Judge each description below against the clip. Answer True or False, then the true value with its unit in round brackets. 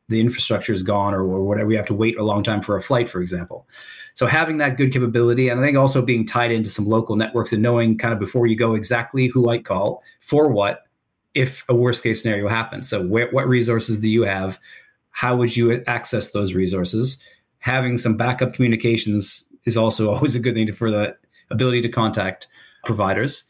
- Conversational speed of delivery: False (210 wpm)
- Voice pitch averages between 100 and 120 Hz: True (115 Hz)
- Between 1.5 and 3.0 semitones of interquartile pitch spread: True (2.5 semitones)